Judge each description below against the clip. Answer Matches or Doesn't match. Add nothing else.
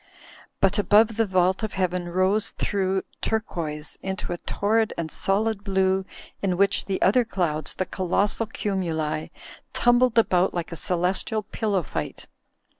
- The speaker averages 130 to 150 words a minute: Matches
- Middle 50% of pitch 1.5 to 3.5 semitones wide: Matches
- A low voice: Doesn't match